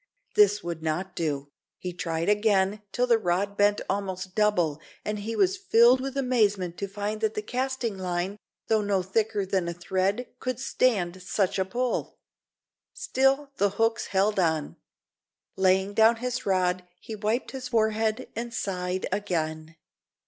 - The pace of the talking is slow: No, average, 155 wpm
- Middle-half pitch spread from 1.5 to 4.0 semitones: Yes, average, 3.6 semitones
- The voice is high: Yes, high, 205 Hz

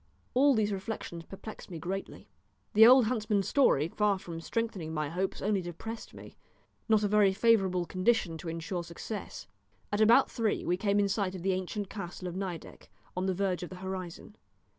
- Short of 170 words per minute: No, average, 185 wpm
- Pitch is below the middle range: No, high, 195 Hz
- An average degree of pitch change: Yes, average, 3.2 semitones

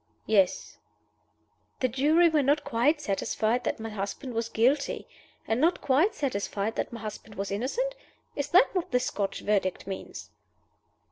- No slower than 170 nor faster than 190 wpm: No, average, 150 wpm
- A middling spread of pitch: No, wide, 5.7 semitones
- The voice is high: Yes, high, 245 Hz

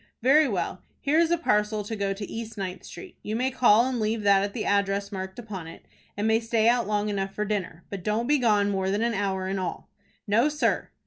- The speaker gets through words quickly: Yes, fast, 240 wpm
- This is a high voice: Yes, high, 210 Hz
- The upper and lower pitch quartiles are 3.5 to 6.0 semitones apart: No, average, 2.9 semitones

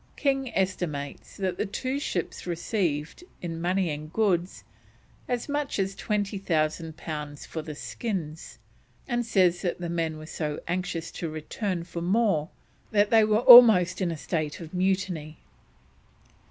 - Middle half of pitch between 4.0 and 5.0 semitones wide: Yes, average, 4.4 semitones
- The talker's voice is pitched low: No, medium, 180 Hz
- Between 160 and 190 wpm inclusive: No, average, 145 wpm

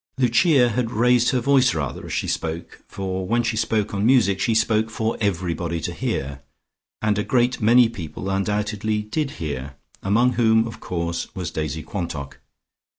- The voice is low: Yes, low, 105 Hz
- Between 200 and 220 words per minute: No, average, 165 wpm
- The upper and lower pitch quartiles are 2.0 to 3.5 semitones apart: No, average, 5.2 semitones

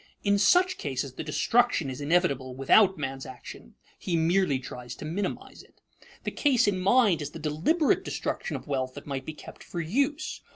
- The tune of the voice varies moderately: No, wide, 7.0 semitones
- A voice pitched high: No, medium, 160 Hz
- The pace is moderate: Yes, average, 180 wpm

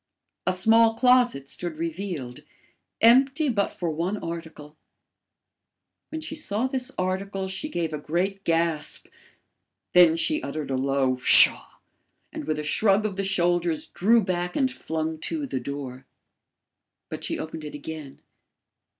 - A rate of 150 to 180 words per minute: No, average, 140 wpm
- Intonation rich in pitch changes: Yes, wide, 5.7 semitones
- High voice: No, medium, 175 Hz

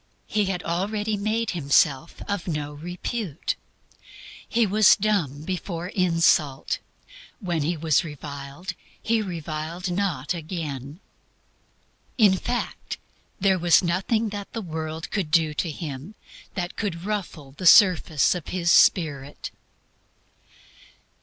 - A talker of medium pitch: Yes, medium, 175 Hz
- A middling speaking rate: No, slow, 115 wpm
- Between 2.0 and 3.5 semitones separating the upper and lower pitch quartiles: No, average, 4.4 semitones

